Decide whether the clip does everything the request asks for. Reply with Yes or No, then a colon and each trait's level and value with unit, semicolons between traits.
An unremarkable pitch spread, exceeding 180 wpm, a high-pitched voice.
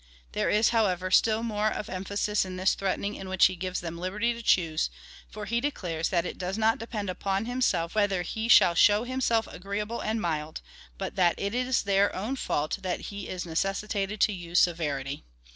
Yes: average, 3.4 semitones; average, 195 wpm; high, 195 Hz